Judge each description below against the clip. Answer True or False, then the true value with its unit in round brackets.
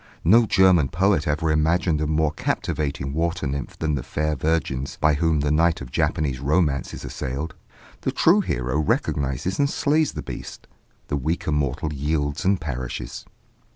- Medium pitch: False (75 Hz)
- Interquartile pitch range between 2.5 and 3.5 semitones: True (2.9 semitones)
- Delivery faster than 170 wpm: False (160 wpm)